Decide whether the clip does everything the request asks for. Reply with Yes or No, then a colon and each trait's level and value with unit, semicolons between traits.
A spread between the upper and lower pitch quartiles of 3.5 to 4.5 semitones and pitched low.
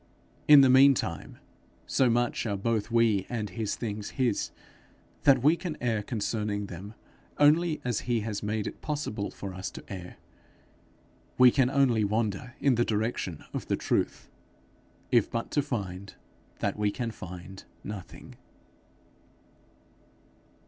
Yes: average, 3.8 semitones; low, 110 Hz